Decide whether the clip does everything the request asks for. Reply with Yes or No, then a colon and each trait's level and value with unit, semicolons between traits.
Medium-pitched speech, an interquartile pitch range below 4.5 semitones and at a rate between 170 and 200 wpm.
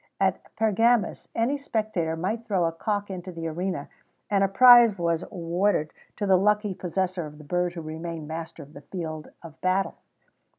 Yes: medium, 180 Hz; average, 4.0 semitones; average, 175 wpm